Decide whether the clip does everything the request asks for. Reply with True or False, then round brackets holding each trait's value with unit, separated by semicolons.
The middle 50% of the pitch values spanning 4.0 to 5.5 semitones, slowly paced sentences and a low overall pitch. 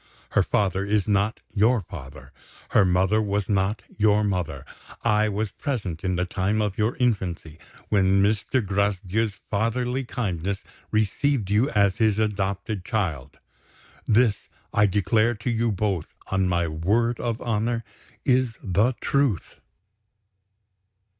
False (2.8 semitones; 130 wpm; 105 Hz)